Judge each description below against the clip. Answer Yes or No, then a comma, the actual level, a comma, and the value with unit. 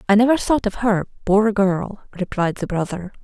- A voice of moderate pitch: No, high, 200 Hz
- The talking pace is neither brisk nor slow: Yes, average, 185 wpm